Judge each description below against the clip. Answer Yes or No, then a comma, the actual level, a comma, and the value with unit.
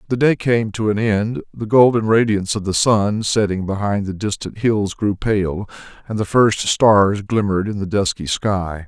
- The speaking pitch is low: Yes, low, 105 Hz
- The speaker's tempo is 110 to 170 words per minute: No, average, 190 wpm